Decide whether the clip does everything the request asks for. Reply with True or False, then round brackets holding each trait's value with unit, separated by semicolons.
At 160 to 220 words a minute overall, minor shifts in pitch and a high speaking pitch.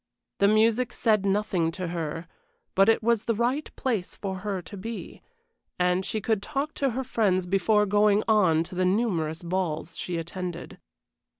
False (170 wpm; 3.8 semitones; 200 Hz)